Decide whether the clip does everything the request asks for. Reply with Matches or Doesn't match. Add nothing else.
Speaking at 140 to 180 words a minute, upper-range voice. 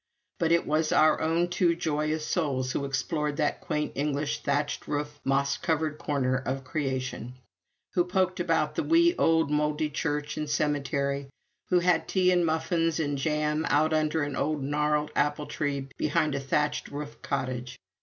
Doesn't match